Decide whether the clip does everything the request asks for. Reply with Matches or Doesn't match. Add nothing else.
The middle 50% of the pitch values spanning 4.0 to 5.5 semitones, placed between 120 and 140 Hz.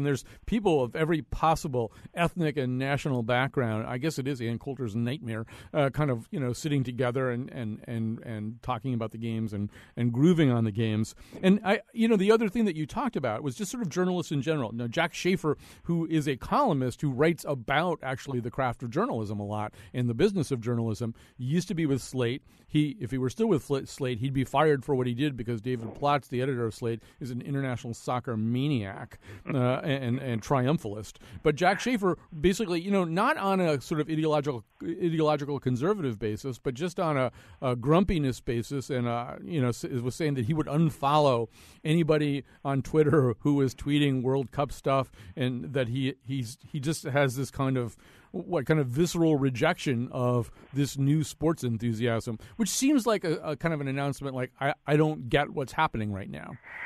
Matches